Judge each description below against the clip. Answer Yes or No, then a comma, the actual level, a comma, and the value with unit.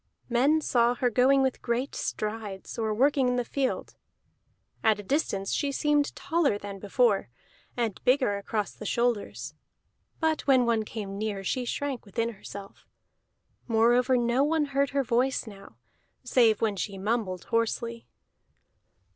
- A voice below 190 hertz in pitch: No, high, 235 Hz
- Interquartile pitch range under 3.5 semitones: No, average, 4.0 semitones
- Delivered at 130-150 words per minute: Yes, average, 145 wpm